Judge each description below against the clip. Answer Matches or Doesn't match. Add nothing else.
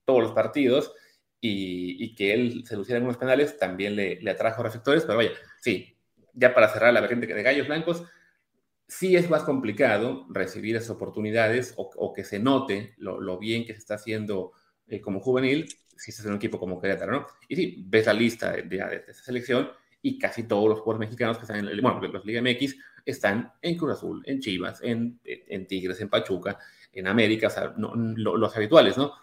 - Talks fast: Matches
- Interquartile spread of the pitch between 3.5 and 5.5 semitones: Matches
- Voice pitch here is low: Matches